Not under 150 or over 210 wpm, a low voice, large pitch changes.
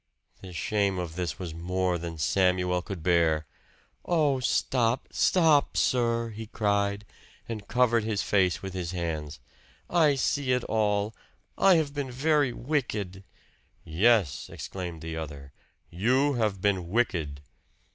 No: slow, 135 wpm; low, 100 Hz; wide, 5.9 semitones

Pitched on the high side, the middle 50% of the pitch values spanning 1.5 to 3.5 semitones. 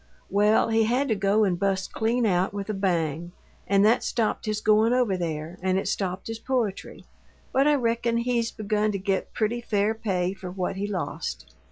Yes: high, 205 Hz; average, 3.2 semitones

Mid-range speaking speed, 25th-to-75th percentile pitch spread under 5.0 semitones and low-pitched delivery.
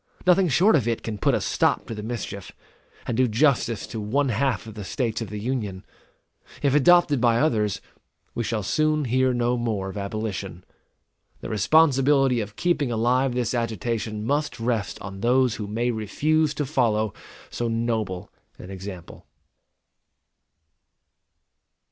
Yes: average, 150 wpm; average, 4.0 semitones; low, 115 Hz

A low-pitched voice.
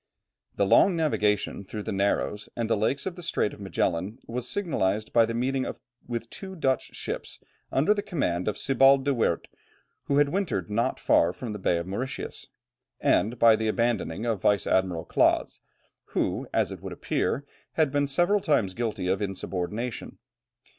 Yes: low, 115 Hz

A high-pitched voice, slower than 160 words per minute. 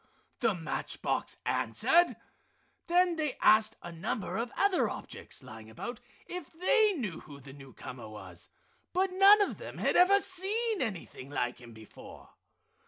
Yes: high, 240 Hz; average, 150 wpm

